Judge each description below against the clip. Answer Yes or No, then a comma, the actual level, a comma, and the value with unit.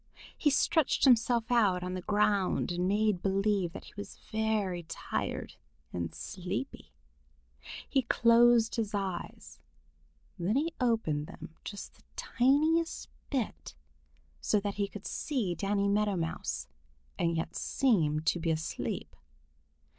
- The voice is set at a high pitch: Yes, high, 205 Hz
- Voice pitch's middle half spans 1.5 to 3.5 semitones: No, average, 4.7 semitones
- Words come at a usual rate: No, slow, 130 wpm